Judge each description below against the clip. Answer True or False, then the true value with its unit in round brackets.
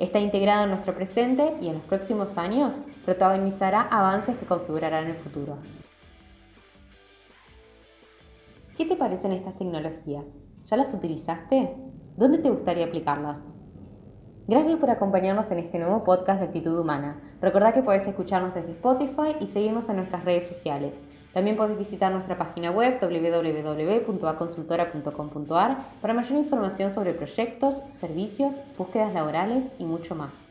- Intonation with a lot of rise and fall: True (5.7 semitones)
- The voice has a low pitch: False (185 Hz)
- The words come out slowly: False (135 wpm)